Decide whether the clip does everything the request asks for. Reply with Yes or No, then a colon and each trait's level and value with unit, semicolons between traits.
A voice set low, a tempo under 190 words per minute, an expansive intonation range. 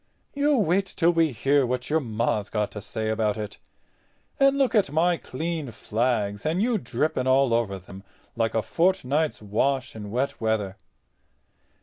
Yes: low, 130 Hz; average, 160 wpm; wide, 7.2 semitones